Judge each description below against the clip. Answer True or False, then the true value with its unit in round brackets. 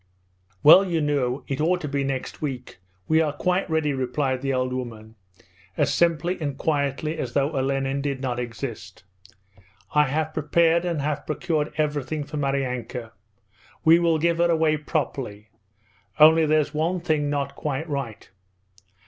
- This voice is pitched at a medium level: True (145 Hz)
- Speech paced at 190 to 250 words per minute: False (155 wpm)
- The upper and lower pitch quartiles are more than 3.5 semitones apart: False (3.0 semitones)